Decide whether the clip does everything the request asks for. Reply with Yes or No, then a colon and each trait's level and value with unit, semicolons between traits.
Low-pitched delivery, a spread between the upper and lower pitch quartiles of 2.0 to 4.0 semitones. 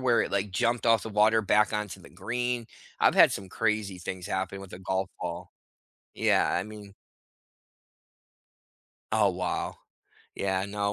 Yes: low, 100 Hz; narrow, 2.6 semitones